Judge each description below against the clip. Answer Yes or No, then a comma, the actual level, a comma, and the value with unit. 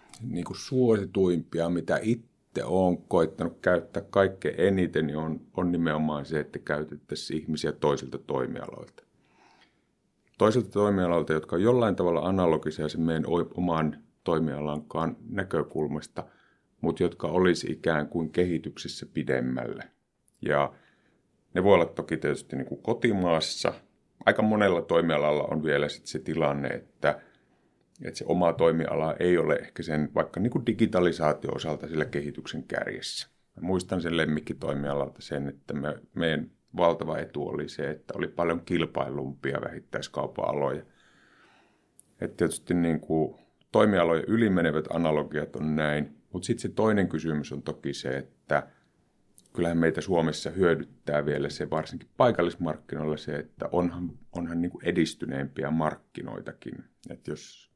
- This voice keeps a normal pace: Yes, average, 130 wpm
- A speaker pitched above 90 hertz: No, very low, 80 Hz